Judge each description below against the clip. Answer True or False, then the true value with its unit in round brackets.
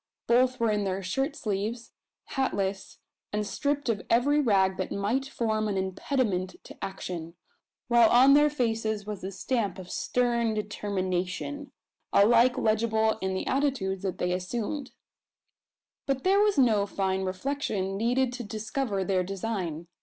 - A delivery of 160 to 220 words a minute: False (145 wpm)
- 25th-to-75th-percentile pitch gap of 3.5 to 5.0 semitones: True (4.7 semitones)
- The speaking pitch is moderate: False (215 Hz)